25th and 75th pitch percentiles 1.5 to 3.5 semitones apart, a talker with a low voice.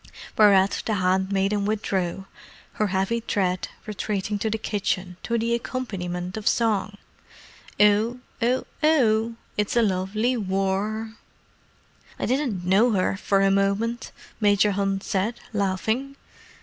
No: average, 2.7 semitones; high, 205 Hz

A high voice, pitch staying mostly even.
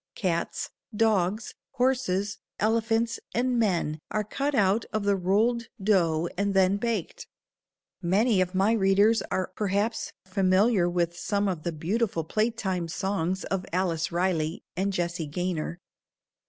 No: high, 195 Hz; average, 3.6 semitones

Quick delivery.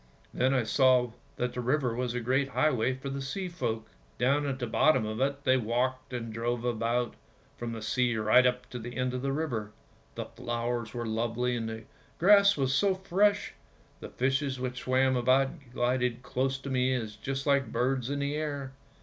No: average, 195 wpm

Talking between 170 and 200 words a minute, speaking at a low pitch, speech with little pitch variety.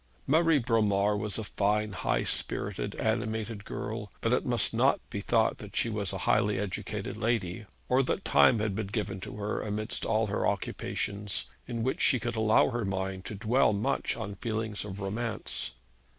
Yes: average, 180 wpm; low, 105 Hz; narrow, 2.1 semitones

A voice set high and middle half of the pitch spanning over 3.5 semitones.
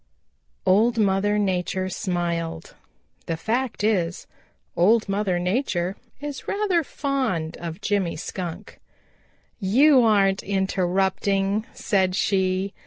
No: high, 195 Hz; average, 3.2 semitones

